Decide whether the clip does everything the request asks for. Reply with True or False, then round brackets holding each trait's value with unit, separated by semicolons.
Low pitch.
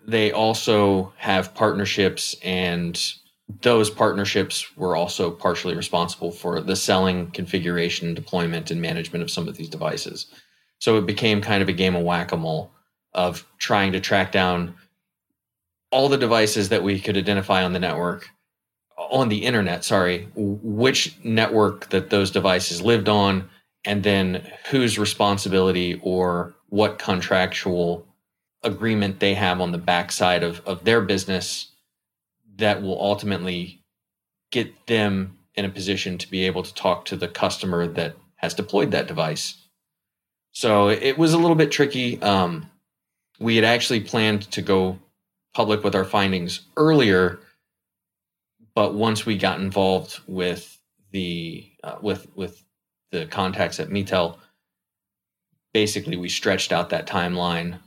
True (95 Hz)